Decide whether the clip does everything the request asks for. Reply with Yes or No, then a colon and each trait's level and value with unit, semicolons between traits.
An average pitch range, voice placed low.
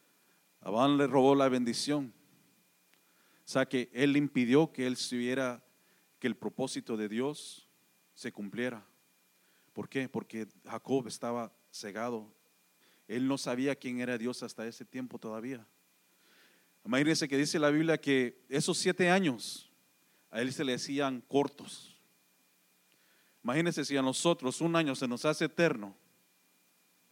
Yes: average, 3.8 semitones; low, 130 Hz